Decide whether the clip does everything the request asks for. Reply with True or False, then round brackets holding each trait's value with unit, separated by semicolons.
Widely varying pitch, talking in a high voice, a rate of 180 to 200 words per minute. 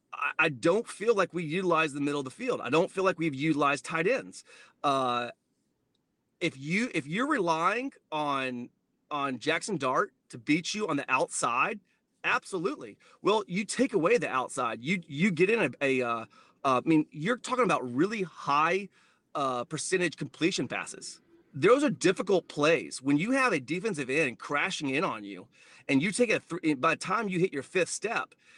False (6.3 semitones; 165 Hz; 185 wpm)